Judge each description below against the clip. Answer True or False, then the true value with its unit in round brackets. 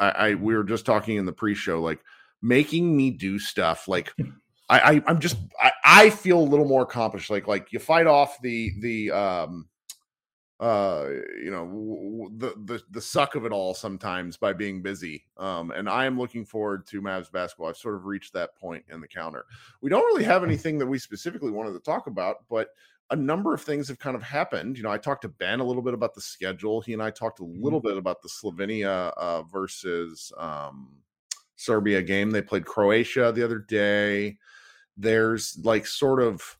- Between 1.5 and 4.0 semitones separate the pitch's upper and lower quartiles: False (4.6 semitones)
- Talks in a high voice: False (110 Hz)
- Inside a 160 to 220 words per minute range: True (205 wpm)